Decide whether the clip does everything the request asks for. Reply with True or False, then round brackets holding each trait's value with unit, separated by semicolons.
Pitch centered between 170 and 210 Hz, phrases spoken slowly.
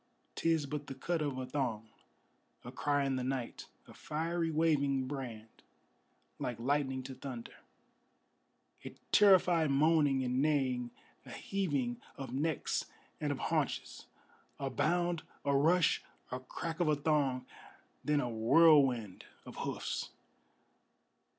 False (140 Hz; 130 wpm)